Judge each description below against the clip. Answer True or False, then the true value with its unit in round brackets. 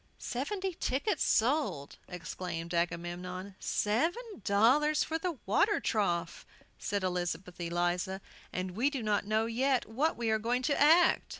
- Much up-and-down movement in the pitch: True (8.0 semitones)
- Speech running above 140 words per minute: False (135 wpm)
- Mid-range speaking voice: False (220 Hz)